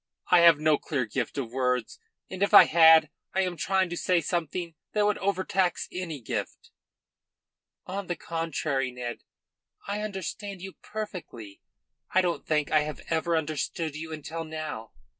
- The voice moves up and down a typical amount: Yes, average, 3.8 semitones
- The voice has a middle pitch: Yes, medium, 165 Hz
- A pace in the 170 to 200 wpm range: No, average, 160 wpm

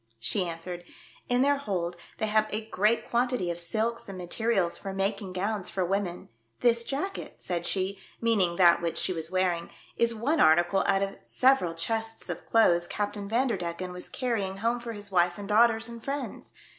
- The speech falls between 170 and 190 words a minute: Yes, average, 180 wpm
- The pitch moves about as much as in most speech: Yes, average, 4.4 semitones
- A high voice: Yes, high, 200 Hz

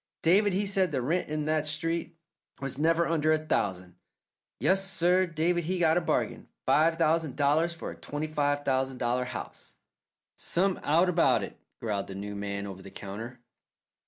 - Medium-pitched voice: Yes, medium, 155 Hz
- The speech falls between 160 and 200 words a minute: Yes, average, 175 wpm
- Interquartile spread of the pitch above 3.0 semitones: Yes, average, 5.0 semitones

